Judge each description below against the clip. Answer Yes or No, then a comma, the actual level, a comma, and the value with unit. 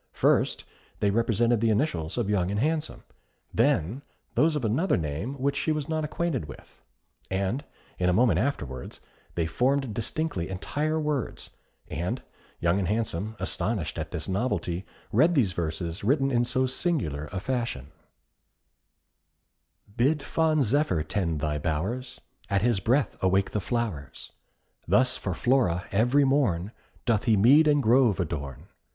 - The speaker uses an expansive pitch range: Yes, wide, 7.4 semitones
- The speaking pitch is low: Yes, low, 110 Hz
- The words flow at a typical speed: Yes, average, 145 wpm